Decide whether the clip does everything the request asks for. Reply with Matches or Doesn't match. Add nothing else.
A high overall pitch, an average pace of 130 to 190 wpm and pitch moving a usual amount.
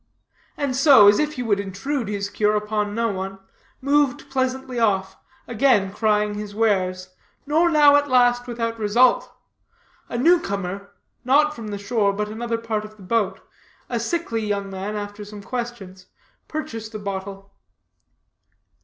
Matches